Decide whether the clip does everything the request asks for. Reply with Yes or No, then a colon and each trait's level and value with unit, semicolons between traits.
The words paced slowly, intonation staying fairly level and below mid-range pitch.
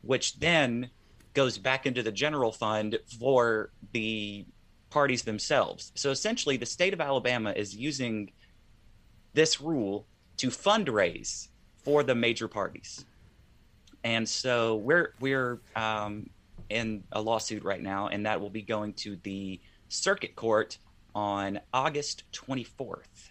No: slow, 130 wpm; average, 4.1 semitones; low, 110 Hz